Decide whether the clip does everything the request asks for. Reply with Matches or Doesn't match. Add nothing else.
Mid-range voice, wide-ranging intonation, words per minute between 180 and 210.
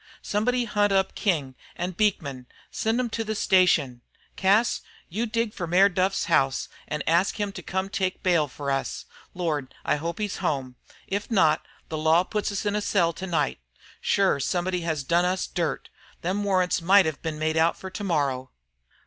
Doesn't match